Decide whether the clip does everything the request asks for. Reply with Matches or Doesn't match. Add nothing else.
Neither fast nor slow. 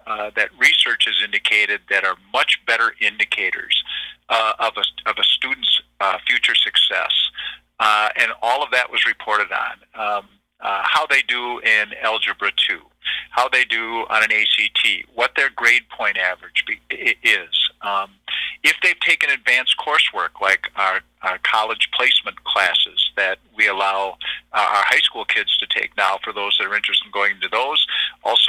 Matches